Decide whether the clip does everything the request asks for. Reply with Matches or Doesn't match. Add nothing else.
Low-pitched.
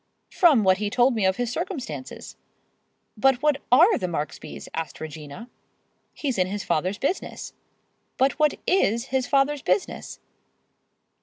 Doesn't match